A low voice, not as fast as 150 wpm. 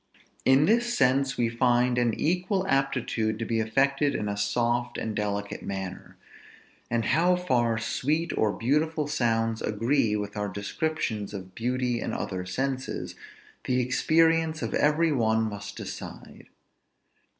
Yes: low, 120 Hz; average, 140 wpm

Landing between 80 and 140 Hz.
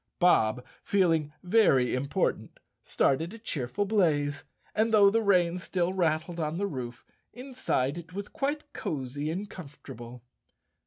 No: medium, 170 Hz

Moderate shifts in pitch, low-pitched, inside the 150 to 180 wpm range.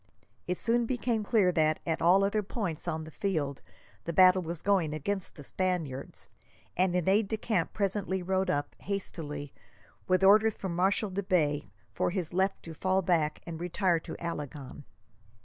No: average, 3.7 semitones; medium, 180 Hz; average, 170 wpm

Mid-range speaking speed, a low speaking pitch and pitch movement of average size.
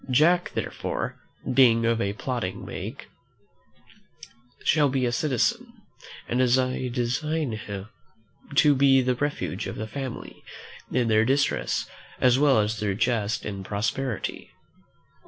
No: slow, 125 wpm; low, 125 Hz; average, 3.8 semitones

